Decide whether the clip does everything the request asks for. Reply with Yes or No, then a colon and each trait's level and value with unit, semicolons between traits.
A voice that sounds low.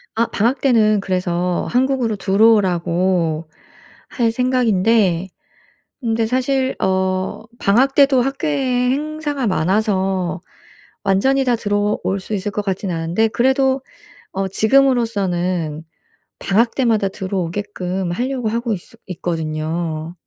No: high, 205 Hz